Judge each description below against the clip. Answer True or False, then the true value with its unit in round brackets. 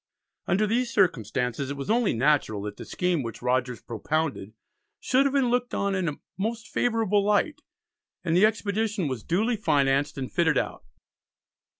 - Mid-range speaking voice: True (180 Hz)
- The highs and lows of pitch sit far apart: True (8.5 semitones)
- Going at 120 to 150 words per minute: False (165 wpm)